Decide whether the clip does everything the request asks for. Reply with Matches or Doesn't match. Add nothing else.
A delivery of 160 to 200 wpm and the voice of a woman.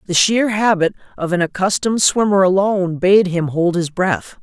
Matches